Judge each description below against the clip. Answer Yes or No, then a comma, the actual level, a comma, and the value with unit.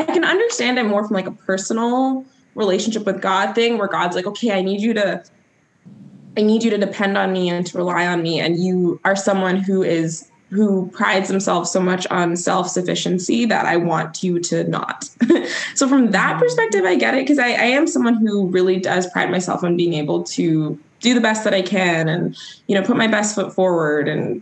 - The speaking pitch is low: No, high, 195 Hz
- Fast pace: Yes, fast, 215 wpm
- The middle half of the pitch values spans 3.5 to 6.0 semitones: Yes, average, 4.2 semitones